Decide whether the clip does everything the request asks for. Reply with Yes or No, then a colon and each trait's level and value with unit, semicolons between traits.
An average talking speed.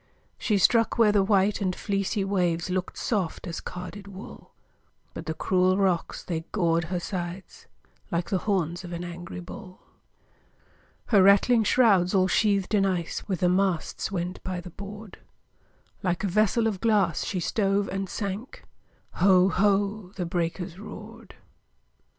Yes: average, 150 wpm